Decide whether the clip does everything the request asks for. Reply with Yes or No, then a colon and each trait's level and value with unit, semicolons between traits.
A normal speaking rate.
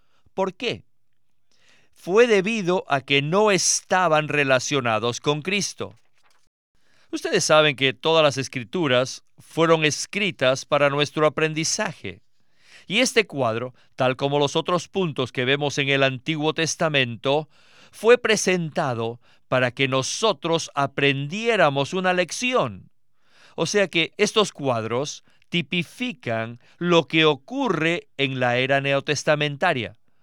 No: slow, 115 wpm